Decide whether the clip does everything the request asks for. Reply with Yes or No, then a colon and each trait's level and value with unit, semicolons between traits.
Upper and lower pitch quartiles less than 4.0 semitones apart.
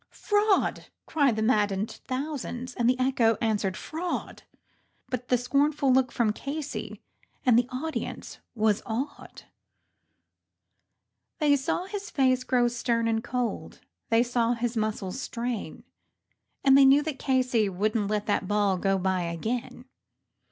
Yes: average, 3.6 semitones